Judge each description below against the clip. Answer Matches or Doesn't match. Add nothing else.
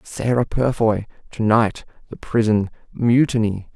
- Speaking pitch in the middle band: Doesn't match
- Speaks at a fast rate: Doesn't match